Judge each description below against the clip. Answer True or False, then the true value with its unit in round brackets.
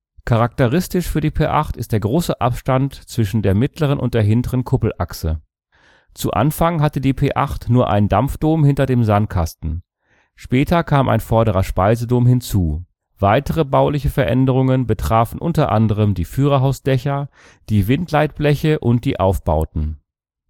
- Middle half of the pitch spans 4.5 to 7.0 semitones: True (5.6 semitones)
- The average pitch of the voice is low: True (125 Hz)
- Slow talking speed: True (130 wpm)